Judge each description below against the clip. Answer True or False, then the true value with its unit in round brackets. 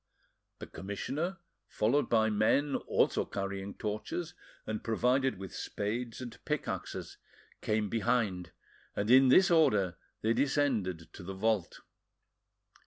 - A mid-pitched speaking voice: False (110 Hz)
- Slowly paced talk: True (115 wpm)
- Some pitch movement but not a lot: True (4.9 semitones)